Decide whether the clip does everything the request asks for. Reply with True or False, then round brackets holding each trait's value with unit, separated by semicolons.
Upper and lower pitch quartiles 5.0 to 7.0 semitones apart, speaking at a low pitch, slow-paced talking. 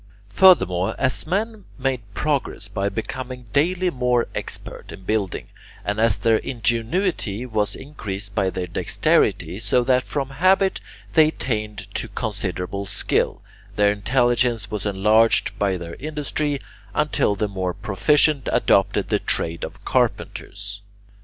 True (5.3 semitones; 110 Hz; 130 wpm)